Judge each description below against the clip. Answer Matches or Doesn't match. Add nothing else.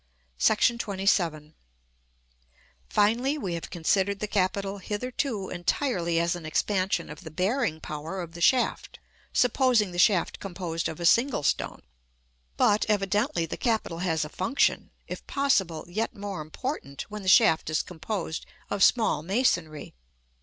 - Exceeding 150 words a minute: Doesn't match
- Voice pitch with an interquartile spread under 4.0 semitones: Doesn't match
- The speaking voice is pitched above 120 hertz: Matches